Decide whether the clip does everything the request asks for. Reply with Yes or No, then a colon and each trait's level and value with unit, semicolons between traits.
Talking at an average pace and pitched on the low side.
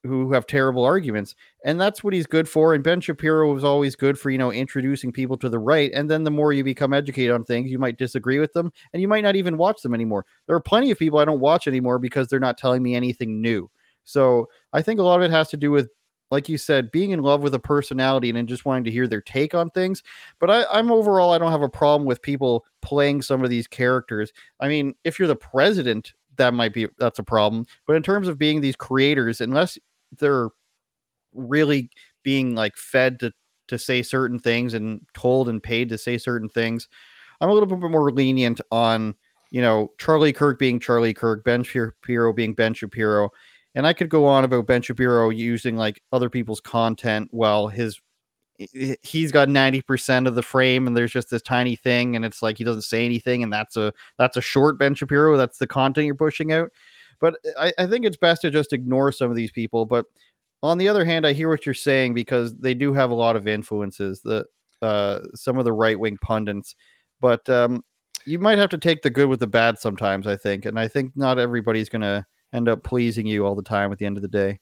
No: fast, 230 wpm; low, 130 Hz